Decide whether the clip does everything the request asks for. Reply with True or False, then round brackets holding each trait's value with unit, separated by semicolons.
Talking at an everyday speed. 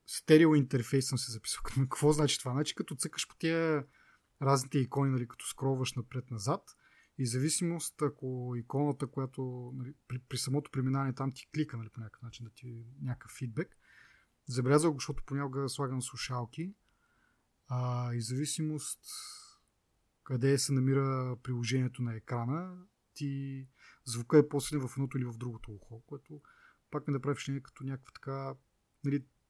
True (155 wpm)